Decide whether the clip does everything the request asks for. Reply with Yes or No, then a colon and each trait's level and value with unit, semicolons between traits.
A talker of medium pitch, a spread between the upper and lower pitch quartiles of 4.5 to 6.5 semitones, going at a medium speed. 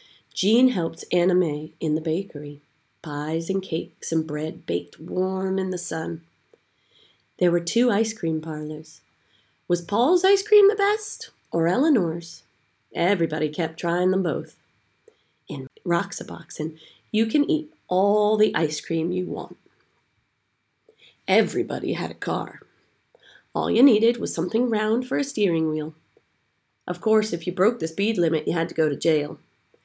Yes: medium, 170 Hz; wide, 5.5 semitones; average, 150 wpm